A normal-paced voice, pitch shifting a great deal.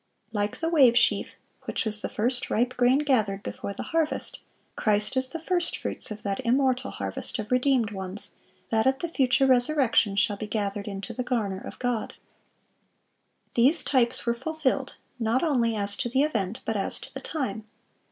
No: average, 180 wpm; average, 4.1 semitones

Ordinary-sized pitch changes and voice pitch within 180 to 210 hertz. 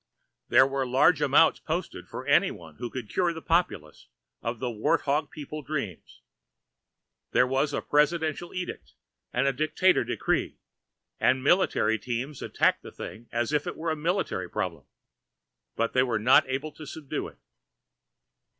No: average, 4.3 semitones; low, 135 Hz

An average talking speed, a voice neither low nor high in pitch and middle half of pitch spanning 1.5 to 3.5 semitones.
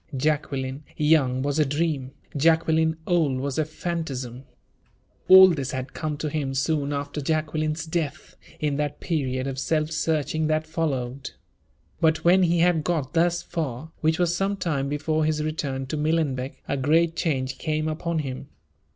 Yes: average, 160 wpm; medium, 155 Hz; average, 2.8 semitones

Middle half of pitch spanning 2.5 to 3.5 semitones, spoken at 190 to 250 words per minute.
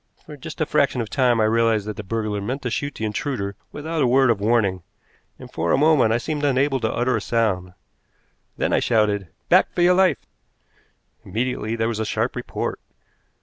No: average, 4.4 semitones; average, 200 wpm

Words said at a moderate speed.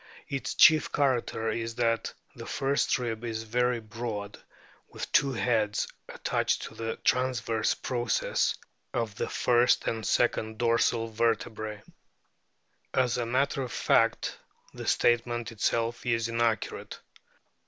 No: slow, 120 wpm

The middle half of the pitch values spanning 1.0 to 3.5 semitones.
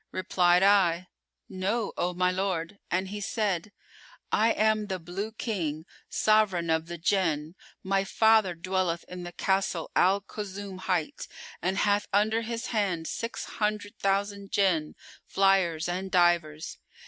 Yes: average, 2.8 semitones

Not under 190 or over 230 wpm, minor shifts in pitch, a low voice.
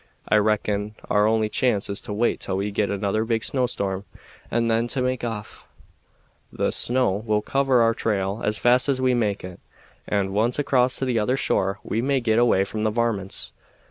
No: average, 195 wpm; average, 3.0 semitones; low, 110 Hz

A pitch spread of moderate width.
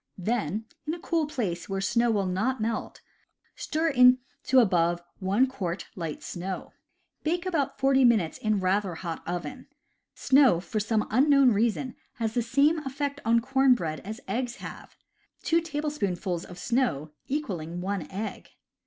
No: wide, 6.2 semitones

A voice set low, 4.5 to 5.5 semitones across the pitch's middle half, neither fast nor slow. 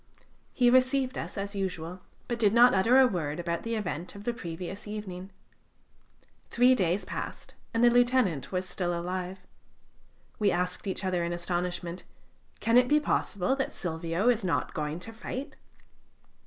No: high, 190 Hz; average, 5.2 semitones; average, 160 wpm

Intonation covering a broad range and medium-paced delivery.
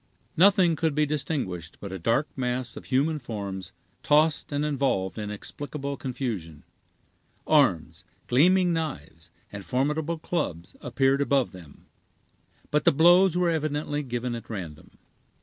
No: wide, 6.8 semitones; slow, 130 wpm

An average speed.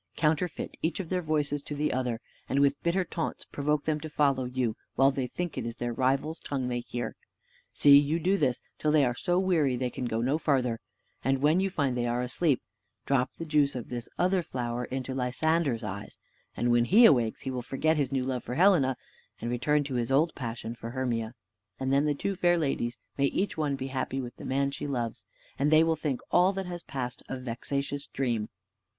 No: fast, 215 wpm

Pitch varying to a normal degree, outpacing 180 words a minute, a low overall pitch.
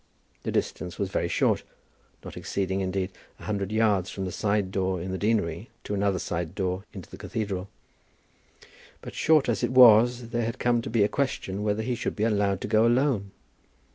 Yes: average, 3.2 semitones; average, 195 wpm; low, 100 Hz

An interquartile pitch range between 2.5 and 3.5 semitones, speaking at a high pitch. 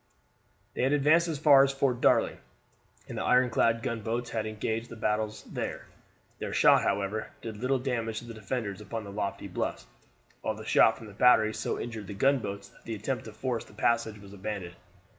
No: average, 2.8 semitones; low, 115 Hz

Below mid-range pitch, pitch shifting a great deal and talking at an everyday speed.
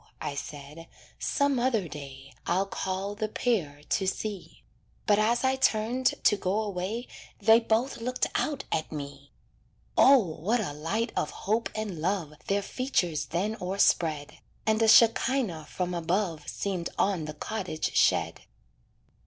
No: high, 195 Hz; wide, 5.7 semitones; average, 145 wpm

